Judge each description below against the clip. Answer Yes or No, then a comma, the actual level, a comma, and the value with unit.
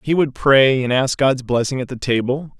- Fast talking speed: Yes, fast, 230 wpm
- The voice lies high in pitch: No, low, 130 Hz